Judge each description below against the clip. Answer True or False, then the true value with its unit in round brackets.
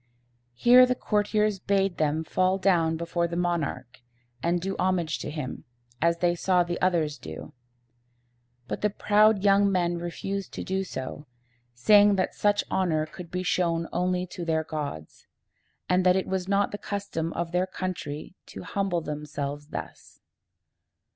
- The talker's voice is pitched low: False (180 Hz)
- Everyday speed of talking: True (155 wpm)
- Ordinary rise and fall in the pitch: True (3.2 semitones)